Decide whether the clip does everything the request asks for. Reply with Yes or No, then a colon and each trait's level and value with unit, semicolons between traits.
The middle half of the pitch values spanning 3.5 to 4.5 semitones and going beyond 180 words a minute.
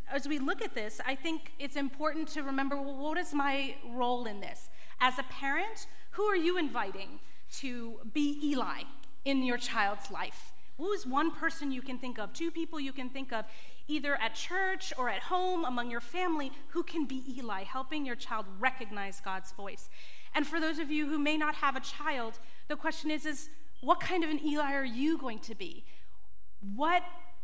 Yes: average, 4.0 semitones; average, 200 wpm